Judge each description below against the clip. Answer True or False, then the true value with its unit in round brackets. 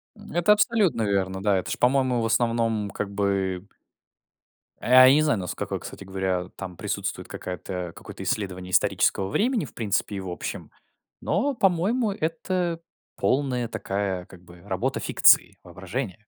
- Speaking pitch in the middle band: False (105 Hz)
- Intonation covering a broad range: True (7.8 semitones)